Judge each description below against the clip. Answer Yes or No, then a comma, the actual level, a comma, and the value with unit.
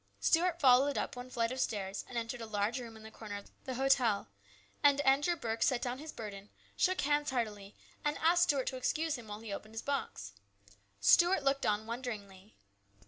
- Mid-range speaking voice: No, high, 245 Hz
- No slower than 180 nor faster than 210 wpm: Yes, average, 195 wpm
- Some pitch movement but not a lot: Yes, average, 4.6 semitones